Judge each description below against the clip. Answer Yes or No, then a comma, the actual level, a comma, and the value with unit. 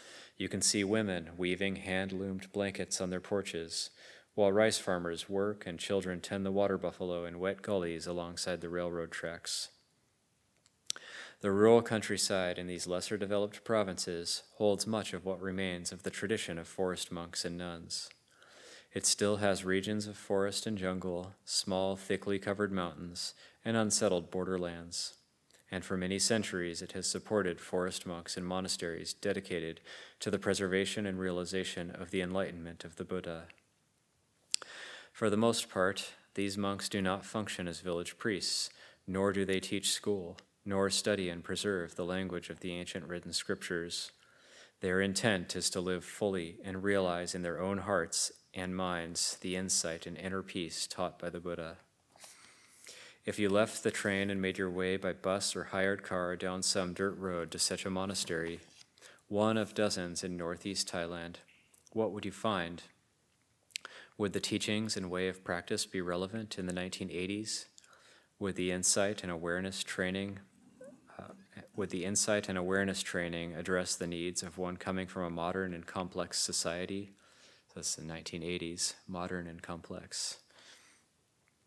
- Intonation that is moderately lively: No, narrow, 2.1 semitones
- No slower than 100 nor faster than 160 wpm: Yes, average, 155 wpm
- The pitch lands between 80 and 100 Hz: Yes, very low, 95 Hz